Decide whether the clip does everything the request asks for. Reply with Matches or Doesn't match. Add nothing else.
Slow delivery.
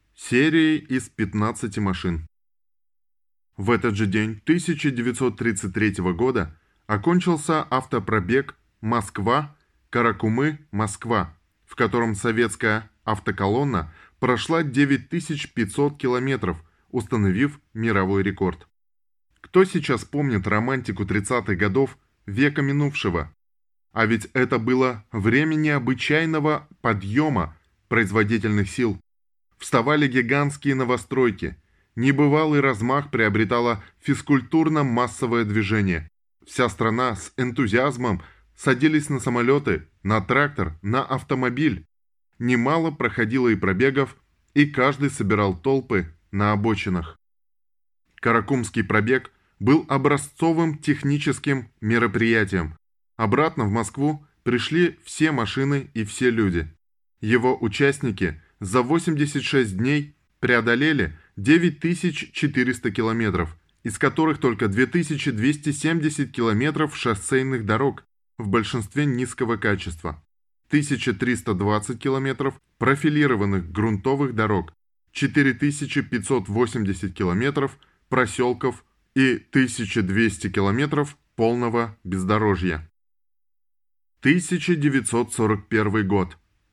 Matches